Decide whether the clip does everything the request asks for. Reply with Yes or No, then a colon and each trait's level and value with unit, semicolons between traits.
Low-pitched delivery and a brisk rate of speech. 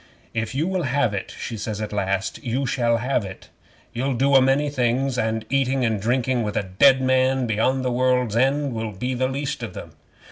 Yes: low, 125 Hz; fast, 210 wpm